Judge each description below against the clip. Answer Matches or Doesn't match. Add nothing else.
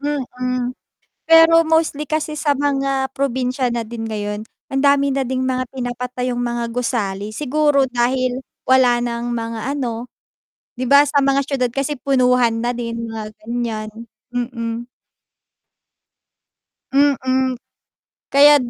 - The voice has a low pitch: Doesn't match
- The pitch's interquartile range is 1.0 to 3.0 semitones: Matches